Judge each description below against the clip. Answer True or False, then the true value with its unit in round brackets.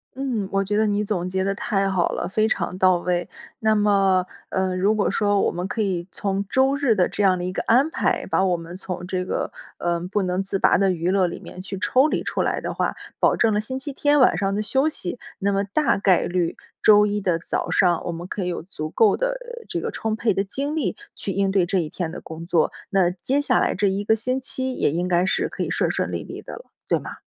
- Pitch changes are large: False (3.2 semitones)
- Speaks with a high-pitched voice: True (195 Hz)